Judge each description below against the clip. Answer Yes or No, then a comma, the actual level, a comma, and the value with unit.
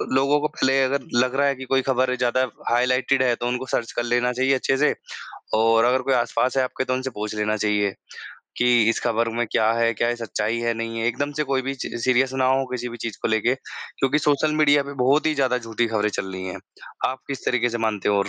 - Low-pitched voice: Yes, low, 125 Hz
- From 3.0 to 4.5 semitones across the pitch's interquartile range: No, narrow, 2.6 semitones